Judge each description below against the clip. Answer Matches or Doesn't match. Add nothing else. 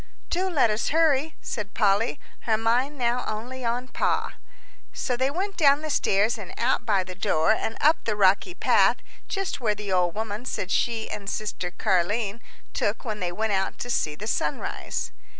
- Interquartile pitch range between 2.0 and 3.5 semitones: Doesn't match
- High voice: Matches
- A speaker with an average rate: Matches